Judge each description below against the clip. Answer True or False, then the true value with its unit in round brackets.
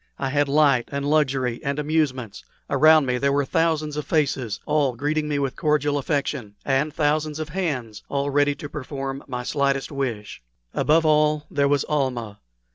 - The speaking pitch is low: False (145 Hz)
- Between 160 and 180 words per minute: True (170 wpm)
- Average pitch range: False (2.1 semitones)